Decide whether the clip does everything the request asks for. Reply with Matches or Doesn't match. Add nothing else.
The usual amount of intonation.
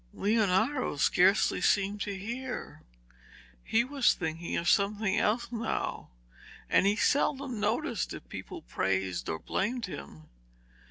Matches